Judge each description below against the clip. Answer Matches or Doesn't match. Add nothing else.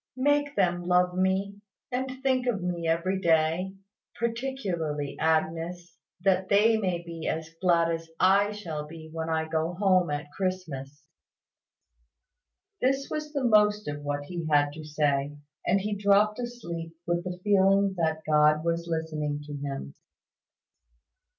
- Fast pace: Doesn't match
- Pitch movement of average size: Matches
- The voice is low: Doesn't match